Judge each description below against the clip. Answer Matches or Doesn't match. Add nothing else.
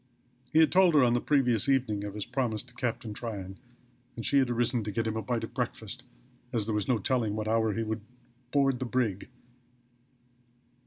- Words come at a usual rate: Doesn't match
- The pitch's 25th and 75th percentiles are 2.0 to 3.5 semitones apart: Matches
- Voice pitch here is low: Matches